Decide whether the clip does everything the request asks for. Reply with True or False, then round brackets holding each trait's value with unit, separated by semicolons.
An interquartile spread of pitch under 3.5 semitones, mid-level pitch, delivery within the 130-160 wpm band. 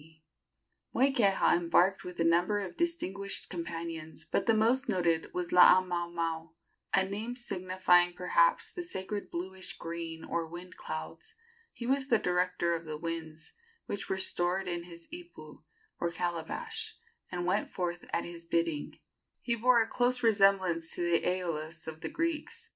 False (4.2 semitones; 180 Hz; 150 wpm)